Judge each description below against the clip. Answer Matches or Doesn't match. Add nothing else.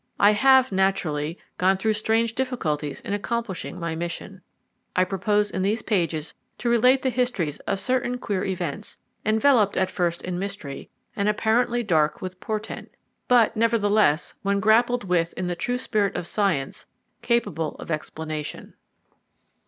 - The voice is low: Doesn't match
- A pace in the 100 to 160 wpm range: Matches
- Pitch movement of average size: Matches